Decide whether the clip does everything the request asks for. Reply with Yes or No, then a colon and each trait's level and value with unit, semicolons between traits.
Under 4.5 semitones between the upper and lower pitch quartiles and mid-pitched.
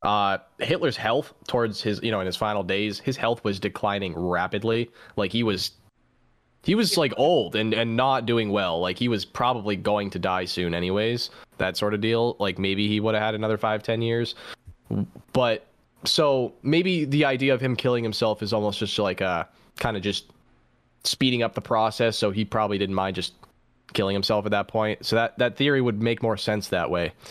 No: narrow, 2.6 semitones; low, 110 Hz